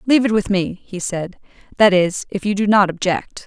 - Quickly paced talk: Yes, fast, 225 wpm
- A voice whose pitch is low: No, high, 195 Hz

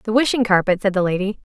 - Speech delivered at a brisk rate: Yes, fast, 245 wpm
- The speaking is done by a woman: Yes, female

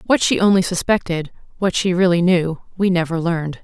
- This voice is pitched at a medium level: Yes, medium, 180 Hz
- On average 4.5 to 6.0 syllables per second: Yes, 5.5 syllables/s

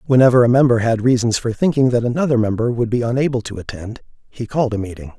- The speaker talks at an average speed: No, fast, 220 wpm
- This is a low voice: Yes, low, 120 Hz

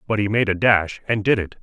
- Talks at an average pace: No, fast, 295 wpm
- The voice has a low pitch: Yes, low, 105 Hz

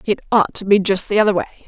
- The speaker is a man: No, female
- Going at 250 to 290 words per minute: Yes, fast, 285 wpm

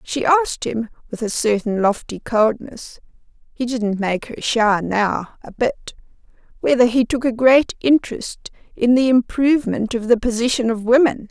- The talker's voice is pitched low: No, high, 235 Hz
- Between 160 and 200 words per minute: No, average, 150 wpm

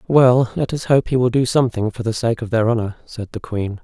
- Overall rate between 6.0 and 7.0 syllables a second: No, 5.7 syllables/s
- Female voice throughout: No, male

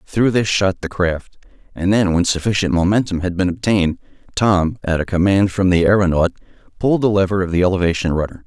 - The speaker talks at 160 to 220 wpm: Yes, average, 190 wpm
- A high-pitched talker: No, very low, 95 Hz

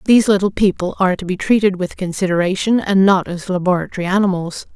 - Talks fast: No, average, 175 wpm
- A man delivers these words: No, female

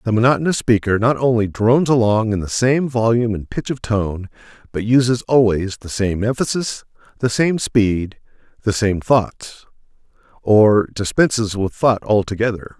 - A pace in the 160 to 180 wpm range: No, average, 145 wpm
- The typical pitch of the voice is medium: No, low, 110 Hz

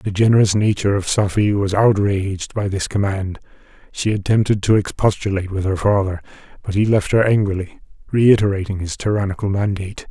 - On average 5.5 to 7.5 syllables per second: Yes, 5.8 syllables/s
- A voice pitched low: Yes, low, 100 Hz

